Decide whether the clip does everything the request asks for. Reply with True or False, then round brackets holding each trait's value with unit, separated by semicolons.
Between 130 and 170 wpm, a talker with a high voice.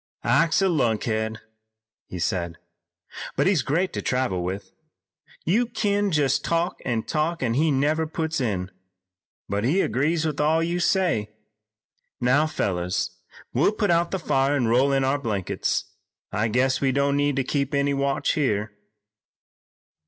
False (150 wpm; 140 Hz)